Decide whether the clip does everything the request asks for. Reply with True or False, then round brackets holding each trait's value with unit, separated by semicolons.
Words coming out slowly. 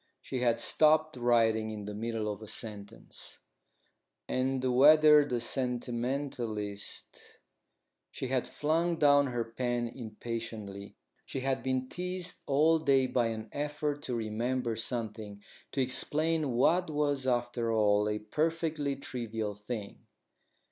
True (125 wpm)